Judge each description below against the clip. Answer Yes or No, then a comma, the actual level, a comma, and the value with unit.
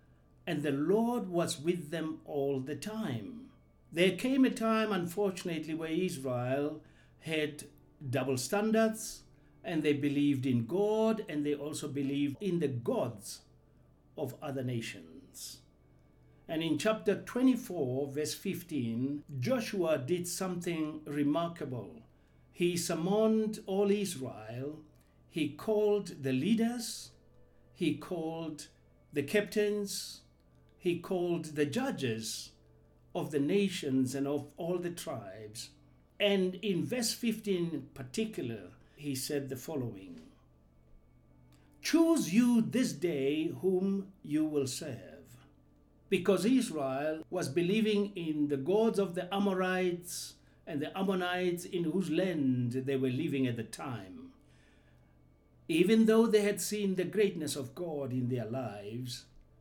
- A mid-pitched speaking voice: Yes, medium, 155 Hz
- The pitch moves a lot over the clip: Yes, wide, 7.2 semitones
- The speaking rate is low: Yes, slow, 120 wpm